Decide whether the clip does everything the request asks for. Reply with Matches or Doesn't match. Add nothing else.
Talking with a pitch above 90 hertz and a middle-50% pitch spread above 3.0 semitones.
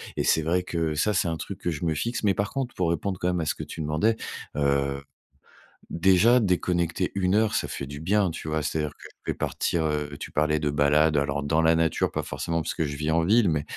Doesn't match